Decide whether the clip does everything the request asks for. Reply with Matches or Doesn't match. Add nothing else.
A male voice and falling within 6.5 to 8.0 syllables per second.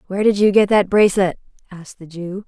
Doesn't match